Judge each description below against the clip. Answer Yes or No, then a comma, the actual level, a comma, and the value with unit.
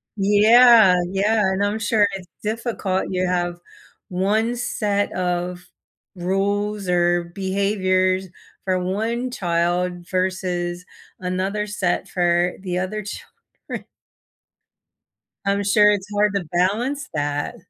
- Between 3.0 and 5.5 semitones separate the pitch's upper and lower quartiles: No, narrow, 2.5 semitones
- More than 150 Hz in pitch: Yes, high, 190 Hz